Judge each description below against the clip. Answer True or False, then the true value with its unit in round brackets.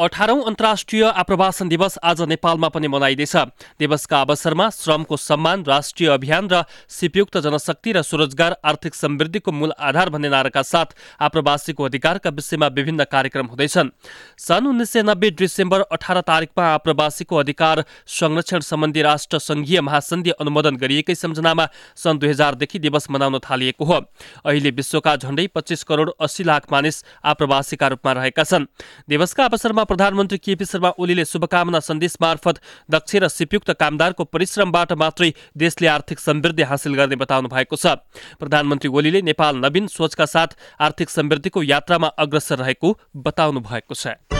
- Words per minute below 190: True (145 wpm)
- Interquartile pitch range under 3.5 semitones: True (3.0 semitones)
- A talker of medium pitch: True (160 Hz)